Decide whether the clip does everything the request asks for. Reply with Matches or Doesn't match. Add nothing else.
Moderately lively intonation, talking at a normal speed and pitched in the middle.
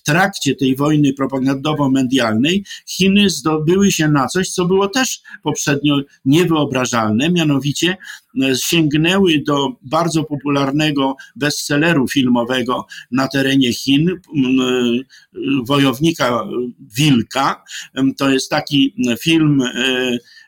Doesn't match